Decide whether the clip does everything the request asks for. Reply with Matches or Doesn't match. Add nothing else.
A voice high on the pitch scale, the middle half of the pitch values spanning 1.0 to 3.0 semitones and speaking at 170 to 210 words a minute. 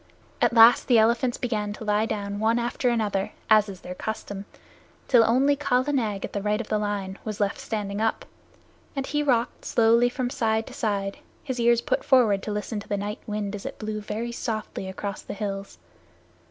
Matches